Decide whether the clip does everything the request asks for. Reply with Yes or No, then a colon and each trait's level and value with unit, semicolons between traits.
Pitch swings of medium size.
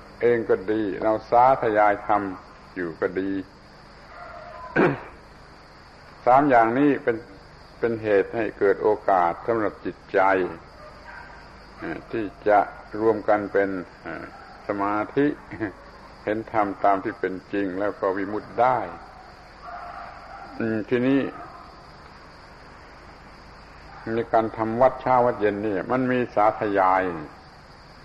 Yes: average, 3.5 semitones